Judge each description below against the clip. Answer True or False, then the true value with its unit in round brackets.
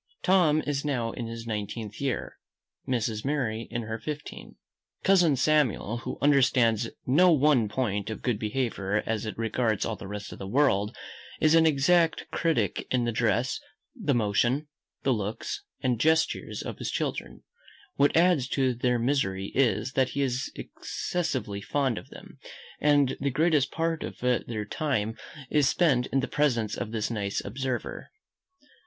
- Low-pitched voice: True (125 Hz)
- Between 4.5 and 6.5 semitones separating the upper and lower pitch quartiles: True (4.8 semitones)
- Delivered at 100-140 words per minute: False (160 wpm)